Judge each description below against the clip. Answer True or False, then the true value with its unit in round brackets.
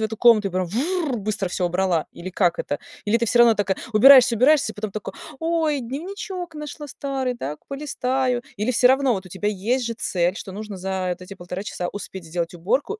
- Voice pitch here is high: True (215 Hz)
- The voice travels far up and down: True (6.0 semitones)